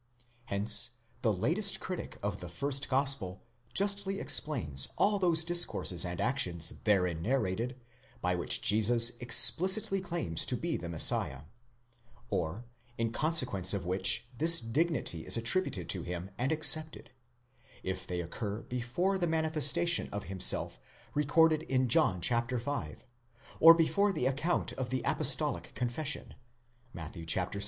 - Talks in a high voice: No, low, 120 Hz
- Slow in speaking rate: Yes, slow, 130 wpm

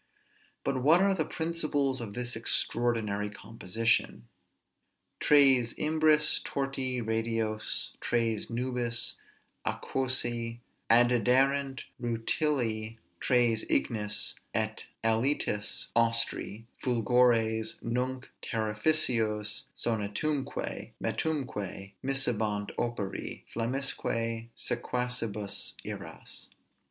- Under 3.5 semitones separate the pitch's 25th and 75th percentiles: Yes, average, 3.0 semitones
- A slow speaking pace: Yes, slow, 75 wpm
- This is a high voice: No, low, 120 Hz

